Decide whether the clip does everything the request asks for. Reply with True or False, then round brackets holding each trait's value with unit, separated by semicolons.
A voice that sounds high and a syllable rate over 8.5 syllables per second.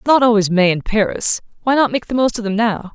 True (220 Hz; 8.7 syllables/s)